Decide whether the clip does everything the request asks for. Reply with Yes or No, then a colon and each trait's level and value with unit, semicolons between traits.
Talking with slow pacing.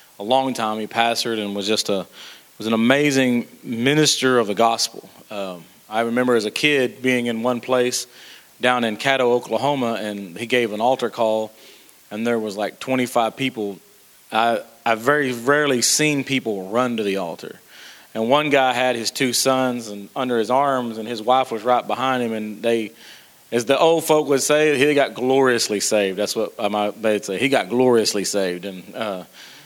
No: average, 190 wpm